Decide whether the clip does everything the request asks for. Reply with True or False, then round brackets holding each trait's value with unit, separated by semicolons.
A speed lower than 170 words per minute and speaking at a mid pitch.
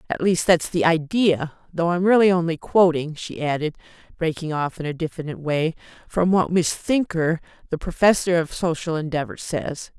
True (160 wpm; 165 Hz)